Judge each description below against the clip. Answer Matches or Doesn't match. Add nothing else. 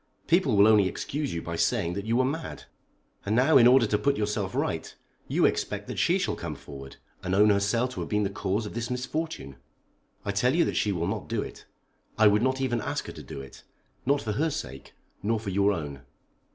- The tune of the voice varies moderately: Matches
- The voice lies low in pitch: Matches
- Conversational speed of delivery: Doesn't match